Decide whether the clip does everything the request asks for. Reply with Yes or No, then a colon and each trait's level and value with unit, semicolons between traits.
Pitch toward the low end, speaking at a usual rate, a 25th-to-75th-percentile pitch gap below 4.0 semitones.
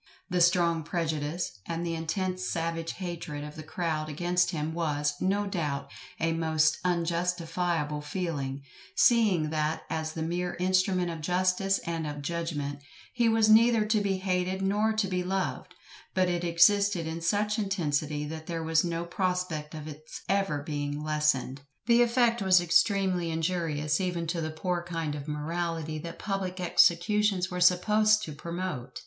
No: medium, 170 Hz; average, 155 wpm; average, 3.0 semitones